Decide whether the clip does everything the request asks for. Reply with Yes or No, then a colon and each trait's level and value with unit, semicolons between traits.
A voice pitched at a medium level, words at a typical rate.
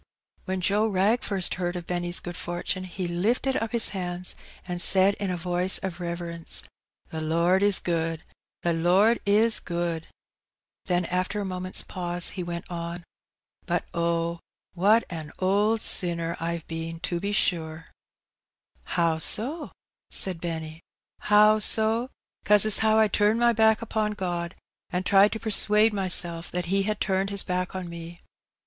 Yes: medium, 180 Hz; average, 170 wpm